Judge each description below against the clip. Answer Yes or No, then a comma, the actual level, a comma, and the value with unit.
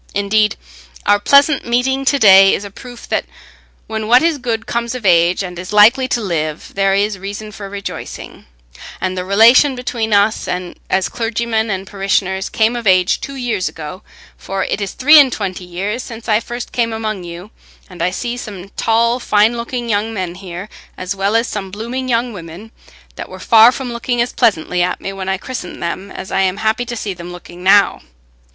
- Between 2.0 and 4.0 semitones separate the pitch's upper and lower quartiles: Yes, average, 3.7 semitones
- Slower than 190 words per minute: No, average, 200 wpm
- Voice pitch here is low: No, high, 210 Hz